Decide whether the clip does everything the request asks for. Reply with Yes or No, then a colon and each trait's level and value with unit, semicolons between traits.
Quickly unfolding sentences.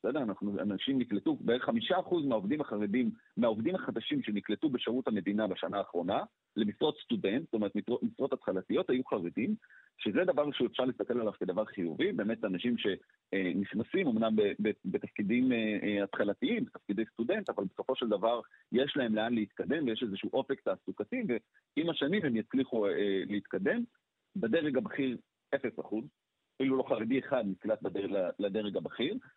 No: average, 135 wpm